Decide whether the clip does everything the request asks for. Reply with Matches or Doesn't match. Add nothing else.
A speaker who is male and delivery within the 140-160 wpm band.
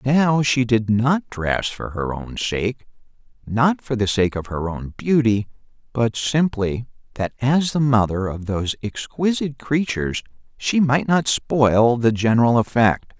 Matches